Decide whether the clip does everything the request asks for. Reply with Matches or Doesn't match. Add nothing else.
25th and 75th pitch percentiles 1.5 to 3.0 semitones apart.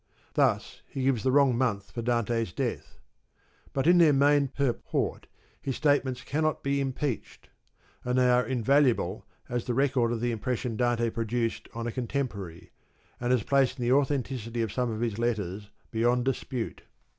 Matches